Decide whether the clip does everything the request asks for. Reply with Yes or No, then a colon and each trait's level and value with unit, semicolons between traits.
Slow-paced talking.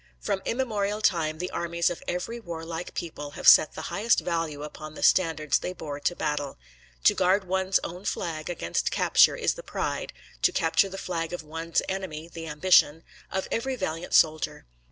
No: average, 175 wpm